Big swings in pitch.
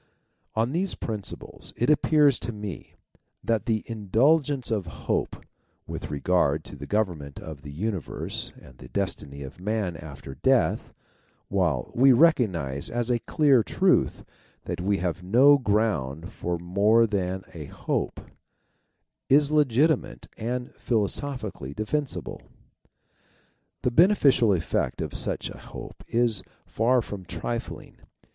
Yes: wide, 6.1 semitones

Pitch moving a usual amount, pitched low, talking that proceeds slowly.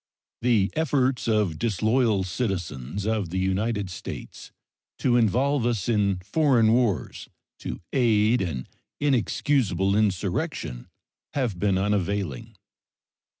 Yes: average, 4.3 semitones; low, 105 Hz; slow, 105 wpm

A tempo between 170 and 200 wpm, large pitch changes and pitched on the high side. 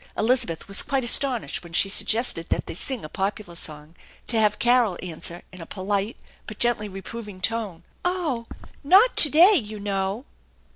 No: average, 175 wpm; average, 4.5 semitones; high, 210 Hz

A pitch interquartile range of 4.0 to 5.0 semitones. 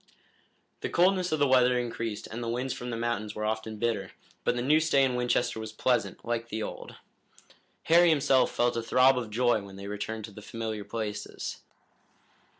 No: average, 2.7 semitones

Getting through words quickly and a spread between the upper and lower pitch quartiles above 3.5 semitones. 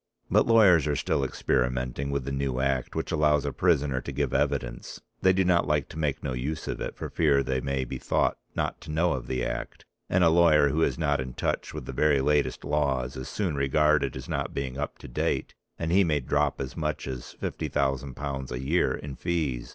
No: fast, 220 wpm; narrow, 2.6 semitones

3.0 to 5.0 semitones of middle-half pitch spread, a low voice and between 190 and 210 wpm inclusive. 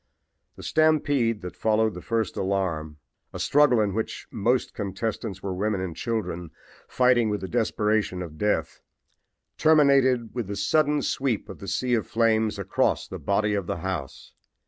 No: average, 4.0 semitones; low, 110 Hz; average, 160 wpm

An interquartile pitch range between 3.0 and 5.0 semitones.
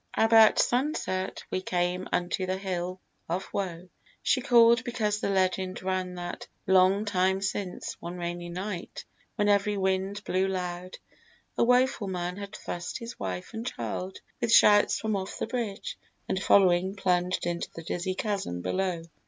No: narrow, 2.5 semitones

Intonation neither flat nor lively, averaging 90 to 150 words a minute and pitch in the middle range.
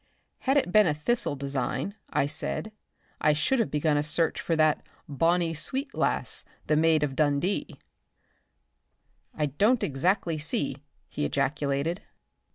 Yes: average, 3.7 semitones; average, 140 wpm; medium, 155 Hz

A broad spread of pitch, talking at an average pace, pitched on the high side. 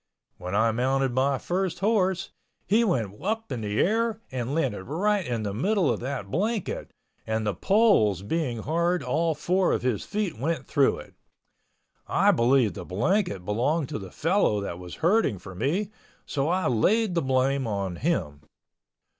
No: wide, 9.0 semitones; average, 170 wpm; medium, 140 Hz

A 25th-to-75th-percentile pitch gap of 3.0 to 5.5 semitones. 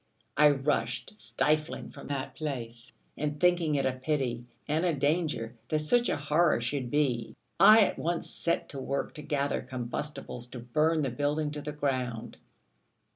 Yes: average, 3.4 semitones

